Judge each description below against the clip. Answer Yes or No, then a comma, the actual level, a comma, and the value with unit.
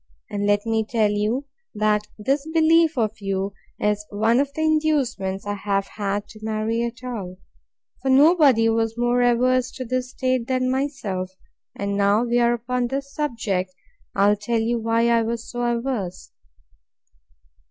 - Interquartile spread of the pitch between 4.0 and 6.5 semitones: No, average, 3.6 semitones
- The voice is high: Yes, high, 230 Hz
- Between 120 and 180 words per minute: Yes, average, 160 wpm